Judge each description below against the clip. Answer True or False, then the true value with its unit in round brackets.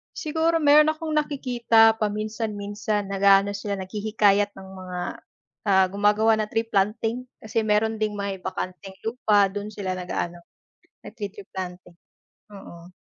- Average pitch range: False (2.3 semitones)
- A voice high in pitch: True (205 Hz)